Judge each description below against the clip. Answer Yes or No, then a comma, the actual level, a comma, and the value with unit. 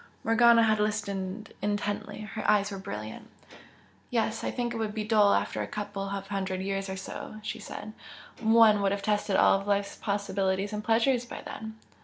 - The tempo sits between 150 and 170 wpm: No, average, 180 wpm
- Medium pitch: No, high, 210 Hz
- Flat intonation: Yes, narrow, 1.9 semitones